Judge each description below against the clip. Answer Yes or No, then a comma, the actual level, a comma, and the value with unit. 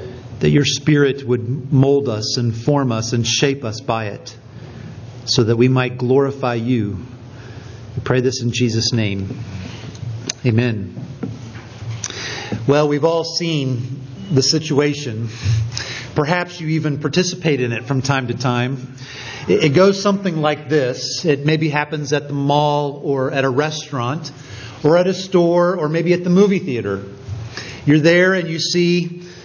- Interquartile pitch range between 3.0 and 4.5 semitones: Yes, average, 4.1 semitones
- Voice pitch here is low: Yes, low, 130 Hz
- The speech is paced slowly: No, average, 150 wpm